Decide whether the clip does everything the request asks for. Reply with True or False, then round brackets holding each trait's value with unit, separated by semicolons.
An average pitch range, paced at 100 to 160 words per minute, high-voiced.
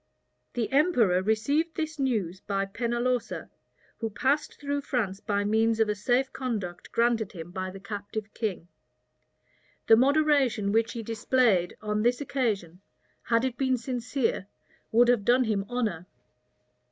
True (4.0 semitones; 140 wpm; 230 Hz)